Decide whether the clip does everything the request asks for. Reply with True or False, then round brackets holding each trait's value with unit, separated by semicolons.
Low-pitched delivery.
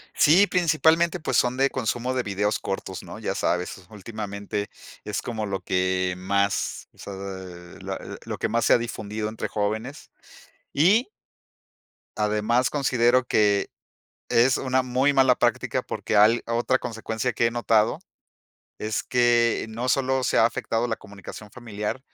True (115 Hz)